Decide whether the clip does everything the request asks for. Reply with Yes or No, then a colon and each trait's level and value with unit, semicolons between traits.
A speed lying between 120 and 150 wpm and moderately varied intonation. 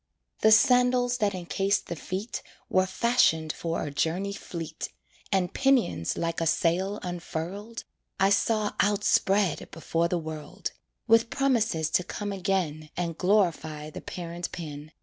Yes: slow, 135 wpm; average, 4.1 semitones